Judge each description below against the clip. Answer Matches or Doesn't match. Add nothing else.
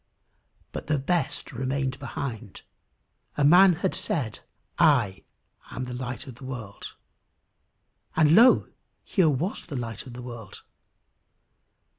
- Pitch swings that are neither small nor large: Matches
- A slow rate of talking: Matches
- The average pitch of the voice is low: Matches